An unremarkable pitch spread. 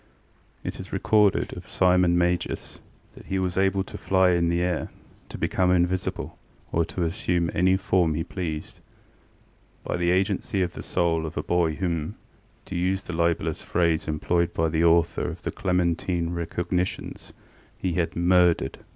No: narrow, 1.6 semitones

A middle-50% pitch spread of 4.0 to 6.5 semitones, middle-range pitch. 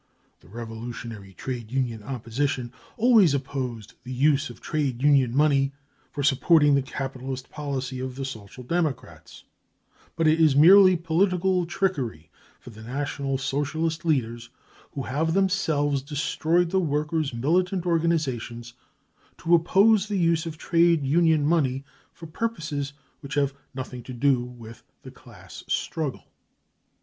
Yes: average, 4.4 semitones; medium, 145 Hz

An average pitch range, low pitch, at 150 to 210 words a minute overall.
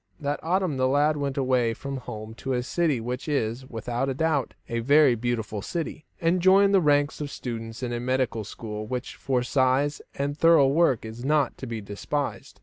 Yes: average, 3.6 semitones; low, 130 Hz; average, 190 wpm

